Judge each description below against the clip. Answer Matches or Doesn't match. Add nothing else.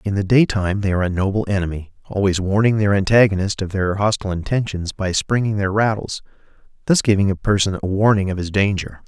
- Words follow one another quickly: Doesn't match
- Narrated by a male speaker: Matches